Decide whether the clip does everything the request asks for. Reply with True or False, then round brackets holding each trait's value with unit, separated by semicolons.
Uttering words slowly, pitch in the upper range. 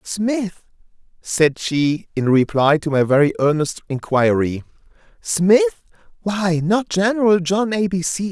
False (125 wpm; 175 Hz)